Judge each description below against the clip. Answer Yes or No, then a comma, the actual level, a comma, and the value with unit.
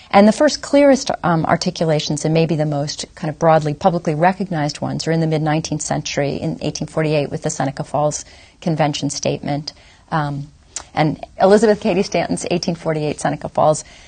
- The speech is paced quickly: No, average, 160 wpm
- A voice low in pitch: No, medium, 155 Hz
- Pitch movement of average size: Yes, average, 3.2 semitones